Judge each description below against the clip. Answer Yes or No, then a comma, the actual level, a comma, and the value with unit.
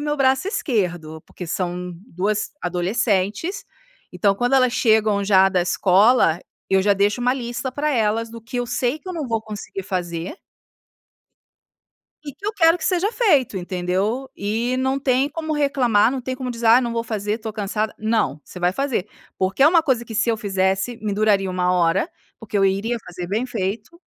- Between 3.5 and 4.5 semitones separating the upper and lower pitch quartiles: No, average, 5.0 semitones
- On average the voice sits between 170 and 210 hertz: No, high, 220 Hz